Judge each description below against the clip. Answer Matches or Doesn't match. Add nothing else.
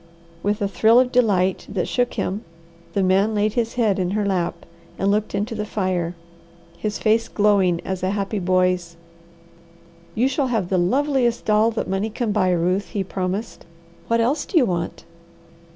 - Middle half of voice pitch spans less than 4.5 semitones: Matches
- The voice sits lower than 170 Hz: Doesn't match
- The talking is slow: Doesn't match